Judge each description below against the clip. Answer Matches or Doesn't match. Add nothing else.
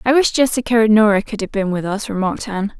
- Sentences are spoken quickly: Matches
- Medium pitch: Doesn't match